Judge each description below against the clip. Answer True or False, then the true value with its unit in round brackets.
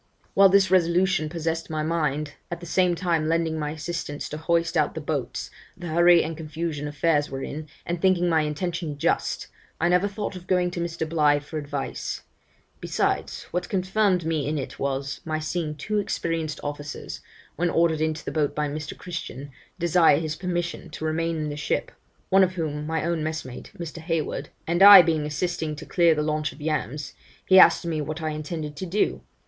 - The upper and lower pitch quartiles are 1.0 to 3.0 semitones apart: True (2.4 semitones)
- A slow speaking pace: False (190 wpm)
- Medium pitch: True (160 Hz)